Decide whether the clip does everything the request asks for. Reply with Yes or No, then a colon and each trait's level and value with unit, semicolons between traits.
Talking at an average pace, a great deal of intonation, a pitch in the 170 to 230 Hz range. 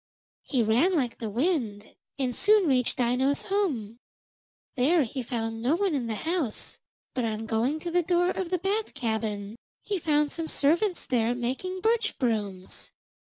No: average, 160 wpm; wide, 7.5 semitones; very high, 265 Hz